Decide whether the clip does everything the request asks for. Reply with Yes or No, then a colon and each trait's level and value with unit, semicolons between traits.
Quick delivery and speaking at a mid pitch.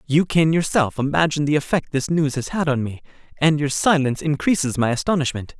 No: average, 195 wpm; medium, 145 Hz